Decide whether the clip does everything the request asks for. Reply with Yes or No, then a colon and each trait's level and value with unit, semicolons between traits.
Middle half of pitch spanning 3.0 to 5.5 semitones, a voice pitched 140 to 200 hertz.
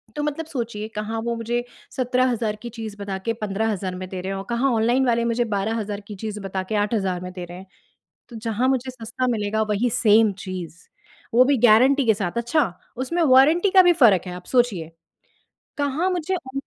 No: average, 4.1 semitones; high, 230 Hz